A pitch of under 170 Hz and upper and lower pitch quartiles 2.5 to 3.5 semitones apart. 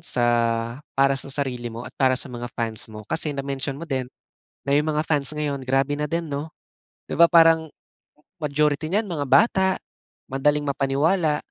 Yes: medium, 140 Hz; average, 3.0 semitones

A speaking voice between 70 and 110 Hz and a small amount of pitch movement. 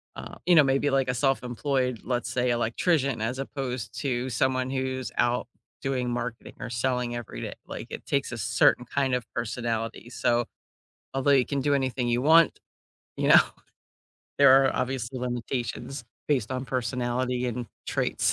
No: low, 125 Hz; narrow, 1.9 semitones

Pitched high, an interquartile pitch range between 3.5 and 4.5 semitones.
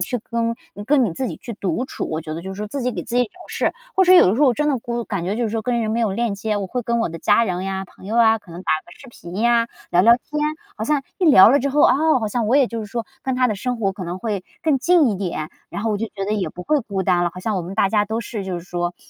Yes: high, 220 Hz; average, 4.2 semitones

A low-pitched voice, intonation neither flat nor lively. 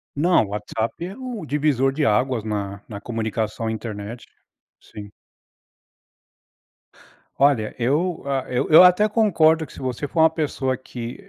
No: low, 130 Hz; wide, 6.1 semitones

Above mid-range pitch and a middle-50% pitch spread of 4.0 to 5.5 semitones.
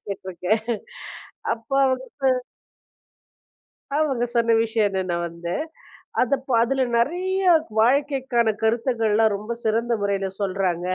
Yes: high, 225 Hz; average, 4.3 semitones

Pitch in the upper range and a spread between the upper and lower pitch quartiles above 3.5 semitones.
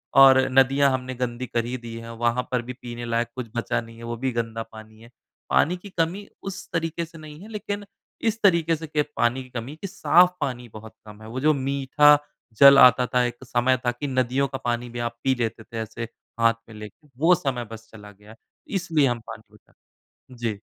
No: low, 125 Hz; average, 4.1 semitones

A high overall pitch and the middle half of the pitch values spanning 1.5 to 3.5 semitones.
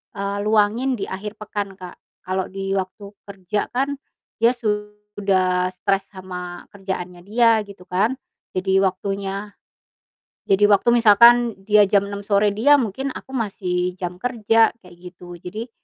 Yes: high, 200 Hz; narrow, 2.5 semitones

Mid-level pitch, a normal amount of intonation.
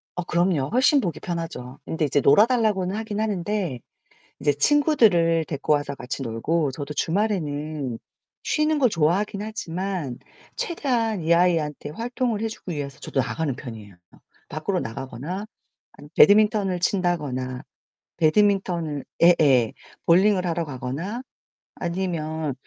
No: medium, 170 Hz; wide, 6.0 semitones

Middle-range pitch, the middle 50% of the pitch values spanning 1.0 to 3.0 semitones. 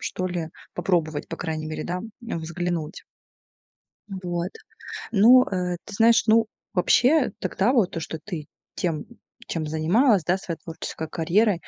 No: medium, 180 Hz; average, 4.3 semitones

